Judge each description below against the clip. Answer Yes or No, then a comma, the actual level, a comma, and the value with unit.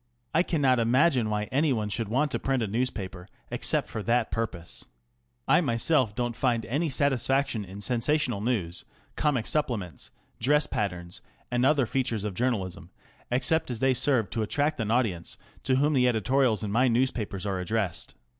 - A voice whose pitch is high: No, low, 120 Hz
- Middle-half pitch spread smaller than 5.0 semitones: Yes, average, 4.1 semitones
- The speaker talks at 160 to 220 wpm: Yes, average, 165 wpm